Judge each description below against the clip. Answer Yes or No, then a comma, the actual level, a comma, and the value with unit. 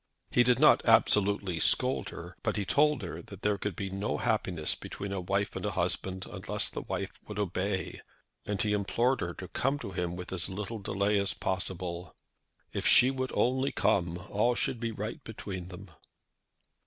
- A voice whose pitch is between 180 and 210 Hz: No, low, 100 Hz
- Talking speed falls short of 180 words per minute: No, average, 185 wpm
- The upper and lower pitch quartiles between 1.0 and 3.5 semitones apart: Yes, average, 2.7 semitones